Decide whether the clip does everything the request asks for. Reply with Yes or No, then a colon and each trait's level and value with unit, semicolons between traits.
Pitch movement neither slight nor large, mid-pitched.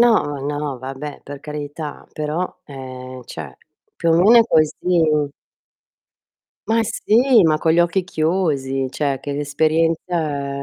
Yes: average, 3.7 semitones; medium, 150 Hz